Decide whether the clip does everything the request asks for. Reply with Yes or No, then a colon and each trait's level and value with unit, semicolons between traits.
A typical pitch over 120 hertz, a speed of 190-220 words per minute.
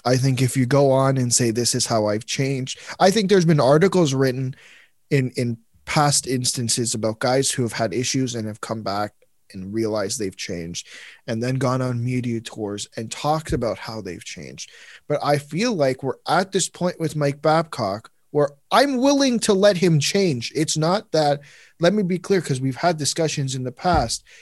Yes: low, 135 Hz; average, 200 wpm